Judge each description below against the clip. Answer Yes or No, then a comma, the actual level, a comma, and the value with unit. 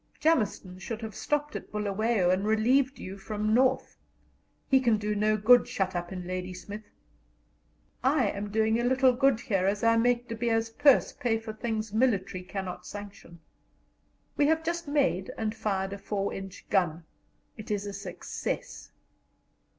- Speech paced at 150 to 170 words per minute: Yes, average, 160 wpm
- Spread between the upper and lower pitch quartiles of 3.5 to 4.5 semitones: Yes, average, 3.8 semitones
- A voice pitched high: Yes, high, 215 Hz